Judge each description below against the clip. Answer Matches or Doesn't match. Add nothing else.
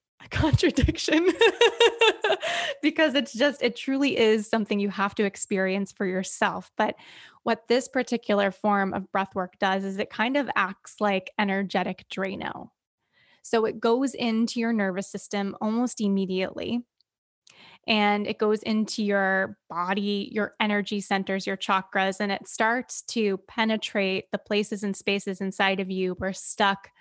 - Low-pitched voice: Doesn't match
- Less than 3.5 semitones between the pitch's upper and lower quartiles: Matches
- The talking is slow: Doesn't match